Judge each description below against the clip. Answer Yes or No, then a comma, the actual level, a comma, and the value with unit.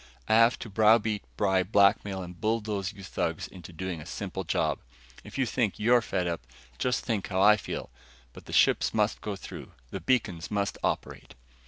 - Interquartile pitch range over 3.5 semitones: No, average, 2.8 semitones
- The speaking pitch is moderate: No, low, 105 Hz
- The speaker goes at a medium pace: Yes, average, 185 wpm